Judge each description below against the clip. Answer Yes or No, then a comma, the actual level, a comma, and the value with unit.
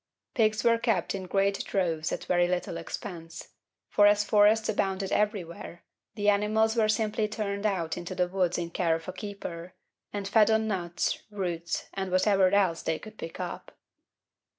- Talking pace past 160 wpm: Yes, average, 170 wpm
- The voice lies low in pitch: No, high, 195 Hz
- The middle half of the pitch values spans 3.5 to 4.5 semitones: No, average, 3.1 semitones